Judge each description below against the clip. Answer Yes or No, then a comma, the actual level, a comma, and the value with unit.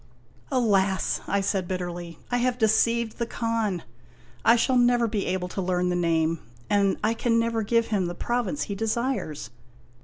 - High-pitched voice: Yes, high, 215 Hz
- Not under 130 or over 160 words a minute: No, average, 185 wpm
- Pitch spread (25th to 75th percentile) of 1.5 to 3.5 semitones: No, average, 4.4 semitones